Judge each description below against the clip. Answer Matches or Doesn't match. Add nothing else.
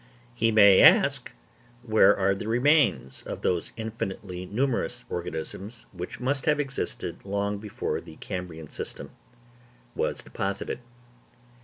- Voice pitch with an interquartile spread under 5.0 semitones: Matches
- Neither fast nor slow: Doesn't match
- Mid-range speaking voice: Doesn't match